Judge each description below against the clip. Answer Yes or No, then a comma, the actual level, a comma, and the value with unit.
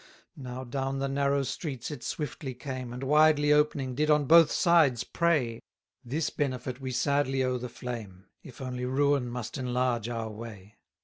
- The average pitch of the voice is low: Yes, low, 130 Hz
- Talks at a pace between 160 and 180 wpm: Yes, average, 170 wpm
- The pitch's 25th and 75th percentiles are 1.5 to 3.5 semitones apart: Yes, average, 2.8 semitones